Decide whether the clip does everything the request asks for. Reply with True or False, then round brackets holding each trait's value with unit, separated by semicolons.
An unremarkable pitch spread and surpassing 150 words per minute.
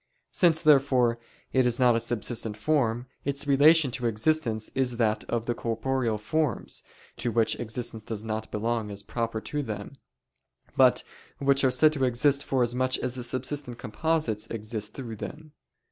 True (3.6 semitones; 160 wpm)